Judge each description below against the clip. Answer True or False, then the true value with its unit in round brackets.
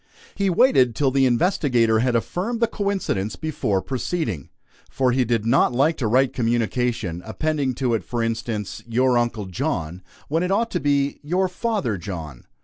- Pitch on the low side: True (125 Hz)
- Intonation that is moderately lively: False (5.8 semitones)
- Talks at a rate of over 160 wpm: True (170 wpm)